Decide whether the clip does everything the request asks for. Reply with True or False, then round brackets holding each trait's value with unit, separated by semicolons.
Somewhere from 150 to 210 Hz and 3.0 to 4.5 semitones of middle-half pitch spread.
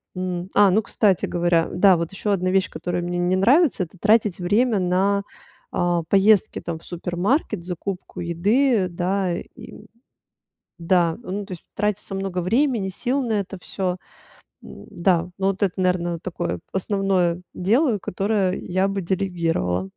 False (185 Hz; 2.4 semitones)